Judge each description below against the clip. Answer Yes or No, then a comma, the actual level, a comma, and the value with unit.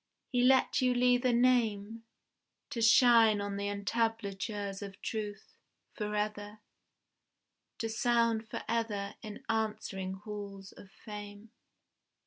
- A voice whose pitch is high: Yes, high, 215 Hz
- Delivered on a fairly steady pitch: Yes, narrow, 2.2 semitones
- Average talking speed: No, slow, 110 wpm